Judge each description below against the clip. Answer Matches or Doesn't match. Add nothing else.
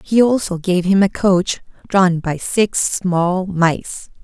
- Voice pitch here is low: Doesn't match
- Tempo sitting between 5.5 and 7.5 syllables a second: Doesn't match